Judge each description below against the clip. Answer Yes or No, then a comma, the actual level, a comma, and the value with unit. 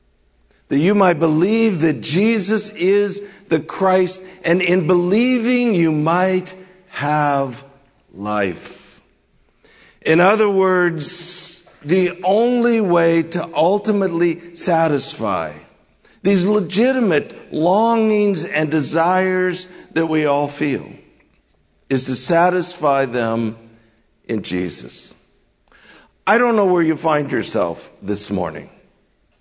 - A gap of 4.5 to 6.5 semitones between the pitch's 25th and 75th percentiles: Yes, average, 5.0 semitones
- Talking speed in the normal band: No, slow, 100 wpm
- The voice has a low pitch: No, medium, 175 Hz